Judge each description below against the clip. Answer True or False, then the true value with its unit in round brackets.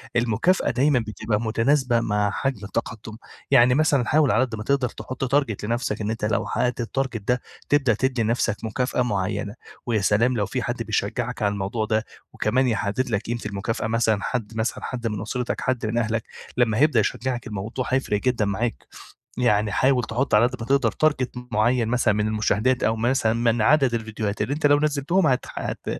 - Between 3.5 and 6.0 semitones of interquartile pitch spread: False (3.0 semitones)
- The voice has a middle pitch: False (115 Hz)